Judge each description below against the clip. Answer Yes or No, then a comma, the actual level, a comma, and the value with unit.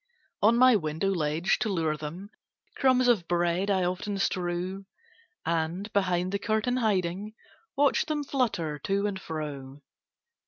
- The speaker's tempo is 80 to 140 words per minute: Yes, slow, 135 wpm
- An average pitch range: Yes, average, 4.2 semitones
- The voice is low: No, high, 190 Hz